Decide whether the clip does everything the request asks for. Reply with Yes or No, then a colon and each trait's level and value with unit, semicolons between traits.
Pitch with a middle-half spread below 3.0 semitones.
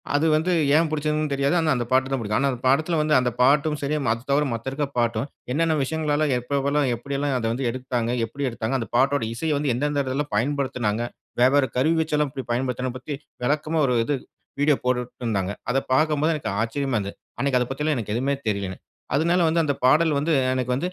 No: average, 3.4 semitones